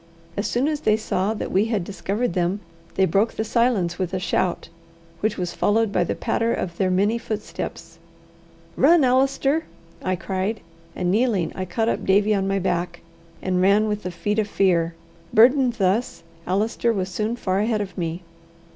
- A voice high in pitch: Yes, high, 200 Hz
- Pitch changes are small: No, average, 3.5 semitones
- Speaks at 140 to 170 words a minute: No, average, 180 wpm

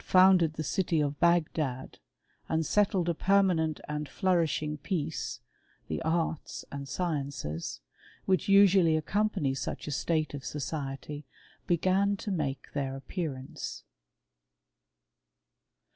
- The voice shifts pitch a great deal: No, average, 4.5 semitones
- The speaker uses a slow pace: Yes, slow, 110 wpm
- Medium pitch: Yes, medium, 160 Hz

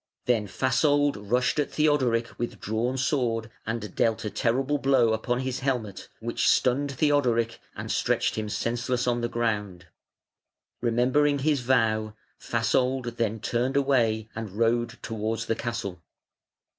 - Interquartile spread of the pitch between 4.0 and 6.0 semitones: No, average, 2.7 semitones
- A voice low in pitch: Yes, low, 120 Hz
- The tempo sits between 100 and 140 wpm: Yes, slow, 135 wpm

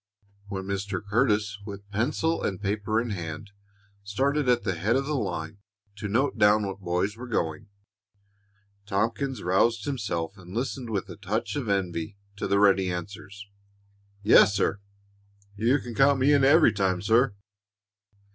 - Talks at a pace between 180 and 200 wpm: No, average, 155 wpm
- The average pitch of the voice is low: Yes, low, 105 Hz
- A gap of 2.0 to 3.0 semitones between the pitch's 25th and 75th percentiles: No, average, 3.6 semitones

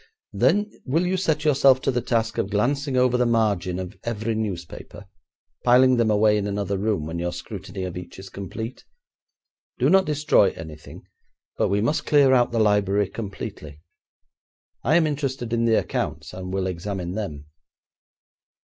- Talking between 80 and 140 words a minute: No, average, 165 wpm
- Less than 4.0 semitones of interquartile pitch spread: No, average, 5.2 semitones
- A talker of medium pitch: No, low, 110 Hz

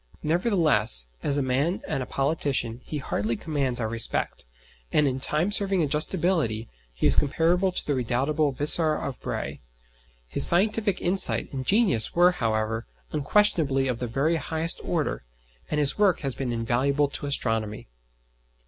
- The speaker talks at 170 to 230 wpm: No, average, 150 wpm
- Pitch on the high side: No, medium, 145 Hz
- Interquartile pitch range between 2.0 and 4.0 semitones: No, wide, 5.4 semitones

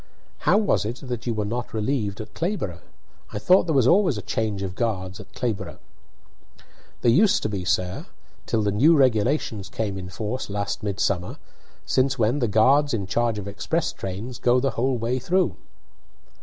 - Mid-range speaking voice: No, low, 110 Hz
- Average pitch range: Yes, average, 4.3 semitones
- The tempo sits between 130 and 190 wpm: Yes, average, 180 wpm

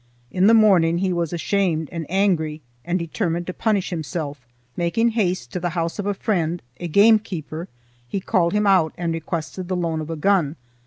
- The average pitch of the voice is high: No, medium, 175 Hz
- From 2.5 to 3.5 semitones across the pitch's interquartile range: Yes, average, 3.1 semitones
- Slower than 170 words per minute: No, average, 190 wpm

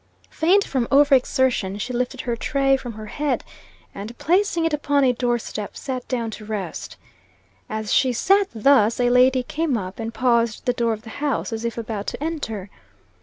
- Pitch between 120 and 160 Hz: No, high, 245 Hz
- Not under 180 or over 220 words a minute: Yes, average, 195 wpm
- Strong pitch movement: No, average, 4.0 semitones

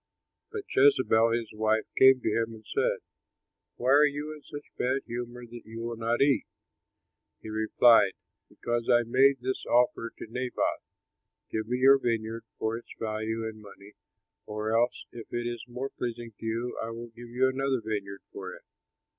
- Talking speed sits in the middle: Yes, average, 175 wpm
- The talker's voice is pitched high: No, low, 120 Hz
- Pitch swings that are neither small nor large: No, narrow, 2.3 semitones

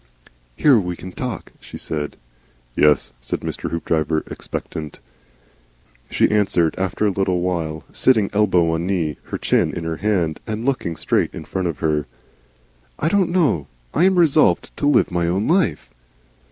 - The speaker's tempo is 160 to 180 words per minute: Yes, average, 165 wpm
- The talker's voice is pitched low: Yes, very low, 90 Hz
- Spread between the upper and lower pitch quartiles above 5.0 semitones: Yes, wide, 5.5 semitones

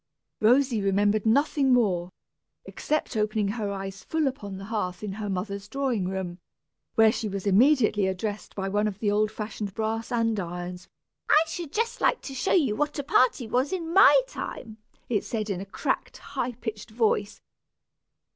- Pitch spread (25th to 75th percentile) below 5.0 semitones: Yes, average, 4.3 semitones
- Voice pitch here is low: No, high, 215 Hz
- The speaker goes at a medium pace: Yes, average, 170 wpm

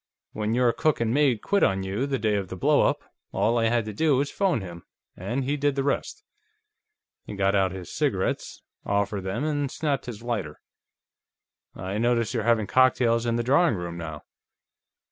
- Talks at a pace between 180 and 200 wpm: Yes, average, 190 wpm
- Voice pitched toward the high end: No, low, 115 Hz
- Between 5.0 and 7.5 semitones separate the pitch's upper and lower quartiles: Yes, average, 5.3 semitones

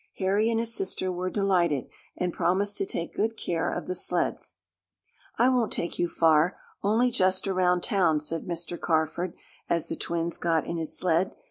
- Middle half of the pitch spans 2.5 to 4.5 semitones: Yes, average, 2.8 semitones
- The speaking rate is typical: Yes, average, 175 wpm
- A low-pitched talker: No, medium, 180 Hz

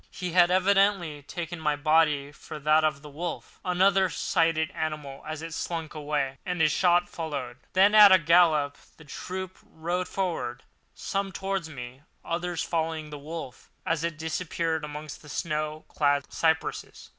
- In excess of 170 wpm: No, average, 155 wpm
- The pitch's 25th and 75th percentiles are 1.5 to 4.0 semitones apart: Yes, average, 2.9 semitones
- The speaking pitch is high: No, medium, 160 Hz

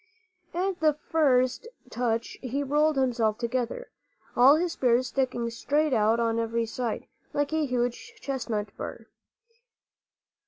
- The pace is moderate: No, slow, 125 wpm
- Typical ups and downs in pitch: Yes, average, 4.0 semitones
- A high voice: Yes, very high, 255 Hz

